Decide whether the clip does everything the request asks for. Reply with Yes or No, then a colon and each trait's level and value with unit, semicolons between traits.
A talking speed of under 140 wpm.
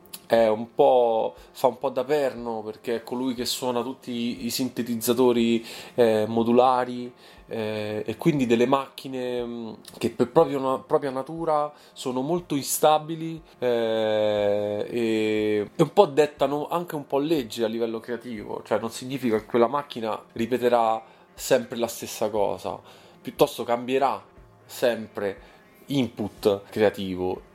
Yes: average, 130 wpm